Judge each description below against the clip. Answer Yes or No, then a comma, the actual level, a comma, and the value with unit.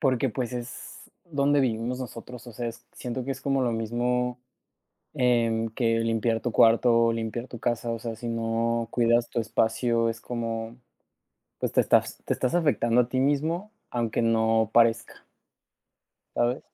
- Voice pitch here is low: Yes, low, 120 Hz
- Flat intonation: Yes, narrow, 1.6 semitones